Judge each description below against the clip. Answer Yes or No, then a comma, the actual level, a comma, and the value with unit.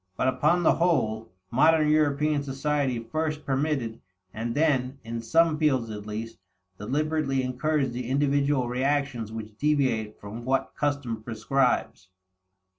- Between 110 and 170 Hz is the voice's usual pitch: Yes, low, 135 Hz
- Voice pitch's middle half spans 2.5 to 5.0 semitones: Yes, average, 4.4 semitones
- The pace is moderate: No, slow, 125 wpm